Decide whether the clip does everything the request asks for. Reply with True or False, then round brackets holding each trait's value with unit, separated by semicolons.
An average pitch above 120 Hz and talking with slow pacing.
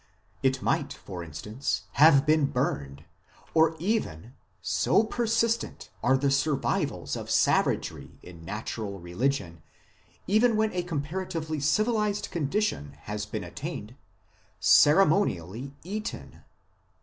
True (140 Hz; 110 wpm)